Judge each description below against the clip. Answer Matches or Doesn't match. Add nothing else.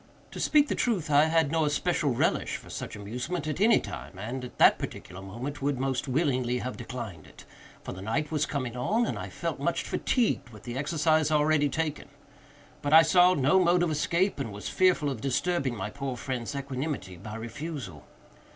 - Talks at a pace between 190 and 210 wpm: Matches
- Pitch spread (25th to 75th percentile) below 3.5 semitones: Doesn't match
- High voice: Doesn't match